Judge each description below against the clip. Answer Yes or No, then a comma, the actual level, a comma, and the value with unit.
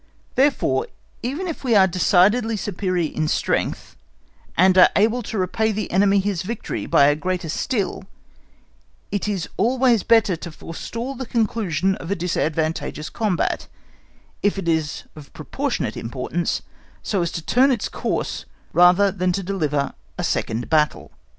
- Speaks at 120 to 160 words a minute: Yes, average, 150 wpm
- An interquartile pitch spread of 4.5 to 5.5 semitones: Yes, average, 4.8 semitones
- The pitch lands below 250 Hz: Yes, high, 190 Hz